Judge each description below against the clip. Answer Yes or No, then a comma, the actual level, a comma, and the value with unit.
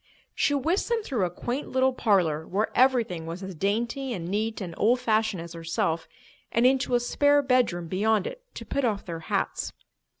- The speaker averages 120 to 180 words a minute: No, average, 190 wpm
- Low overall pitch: No, high, 220 Hz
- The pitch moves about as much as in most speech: No, wide, 6.4 semitones